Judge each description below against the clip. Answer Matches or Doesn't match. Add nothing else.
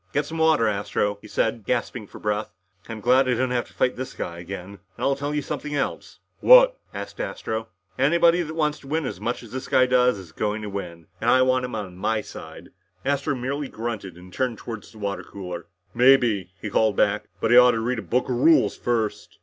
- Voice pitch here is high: Doesn't match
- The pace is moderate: Doesn't match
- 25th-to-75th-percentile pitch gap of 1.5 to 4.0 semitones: Doesn't match